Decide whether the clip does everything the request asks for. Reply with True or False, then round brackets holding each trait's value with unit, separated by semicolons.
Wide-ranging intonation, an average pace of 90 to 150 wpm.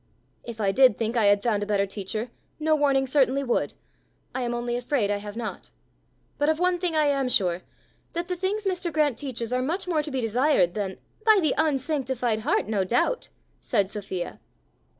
False (6.0 semitones; 200 wpm)